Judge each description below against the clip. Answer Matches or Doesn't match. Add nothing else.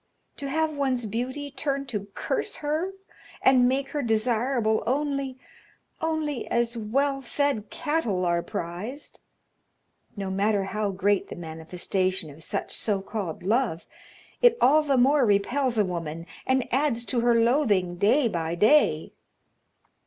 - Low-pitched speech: Doesn't match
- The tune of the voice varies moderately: Doesn't match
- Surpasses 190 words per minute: Doesn't match